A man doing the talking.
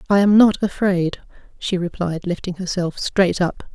No: female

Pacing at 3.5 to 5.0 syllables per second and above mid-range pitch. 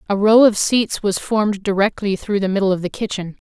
No: 5.6 syllables/s; high, 200 Hz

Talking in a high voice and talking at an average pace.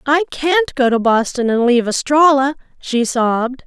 Yes: very high, 265 Hz; average, 165 wpm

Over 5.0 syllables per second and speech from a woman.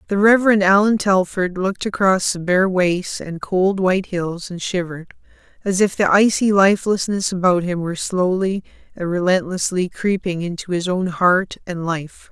No: 4.9 syllables/s; female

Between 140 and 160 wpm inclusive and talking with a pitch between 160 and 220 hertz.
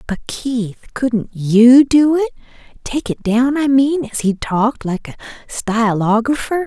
No: average, 145 wpm; high, 240 Hz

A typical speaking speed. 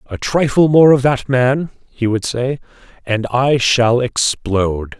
Yes: average, 155 wpm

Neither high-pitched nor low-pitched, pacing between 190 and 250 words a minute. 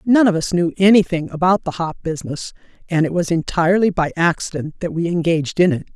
Yes: medium, 170 Hz; average, 200 wpm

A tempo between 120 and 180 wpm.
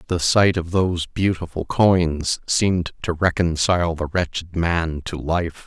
Yes: average, 150 wpm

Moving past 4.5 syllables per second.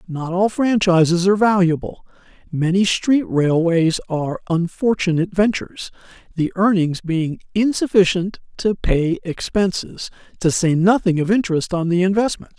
Yes: 4.8 syllables/s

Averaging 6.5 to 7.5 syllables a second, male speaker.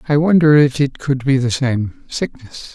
No: 4.4 syllables/s; male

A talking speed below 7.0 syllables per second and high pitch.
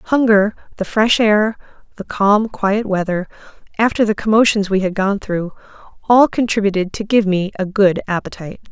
Yes: 5.0 syllables/s; high, 205 Hz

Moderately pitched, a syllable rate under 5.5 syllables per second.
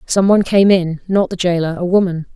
No: medium, 180 Hz; 5.7 syllables/s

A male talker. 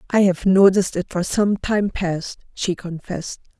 No: female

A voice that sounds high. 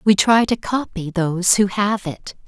Yes: high, 195 Hz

